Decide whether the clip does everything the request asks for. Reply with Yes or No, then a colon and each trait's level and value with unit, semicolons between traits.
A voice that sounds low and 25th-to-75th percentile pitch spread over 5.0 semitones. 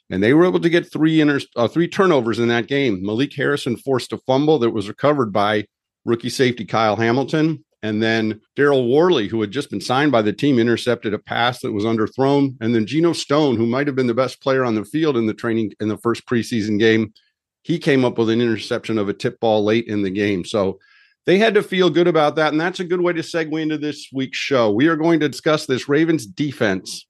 Yes: low, 130 Hz; wide, 5.5 semitones